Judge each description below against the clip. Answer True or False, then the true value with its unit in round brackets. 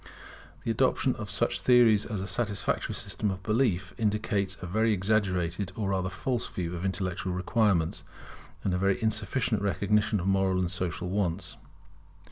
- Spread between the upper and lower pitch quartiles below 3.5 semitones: True (2.6 semitones)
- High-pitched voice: False (95 Hz)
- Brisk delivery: False (155 wpm)